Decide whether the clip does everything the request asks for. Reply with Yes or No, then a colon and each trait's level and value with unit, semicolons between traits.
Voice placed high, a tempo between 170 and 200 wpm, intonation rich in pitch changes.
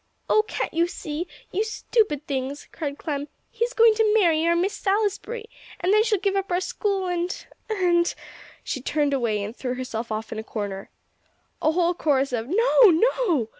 Yes: very high, 345 Hz; average, 185 wpm; wide, 7.0 semitones